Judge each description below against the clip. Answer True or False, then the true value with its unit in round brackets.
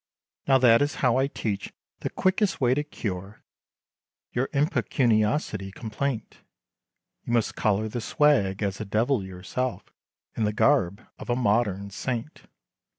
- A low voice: True (115 Hz)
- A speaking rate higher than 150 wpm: False (140 wpm)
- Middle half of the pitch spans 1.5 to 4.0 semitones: False (4.8 semitones)